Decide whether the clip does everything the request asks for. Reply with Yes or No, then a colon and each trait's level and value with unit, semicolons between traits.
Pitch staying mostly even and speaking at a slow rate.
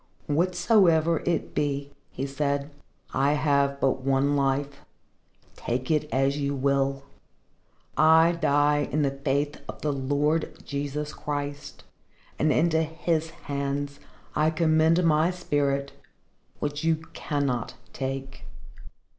Yes: narrow, 2.2 semitones; slow, 115 wpm